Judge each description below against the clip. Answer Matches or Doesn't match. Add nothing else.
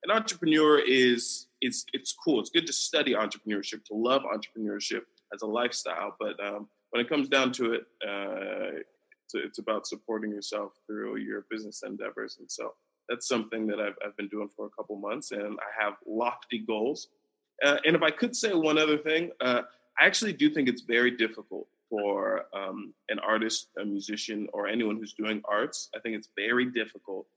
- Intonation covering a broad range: Matches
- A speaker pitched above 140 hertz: Doesn't match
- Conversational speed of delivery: Matches